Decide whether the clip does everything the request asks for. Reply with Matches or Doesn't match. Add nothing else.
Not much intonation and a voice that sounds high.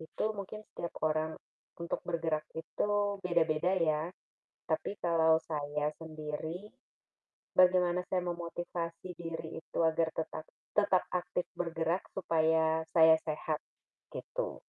Doesn't match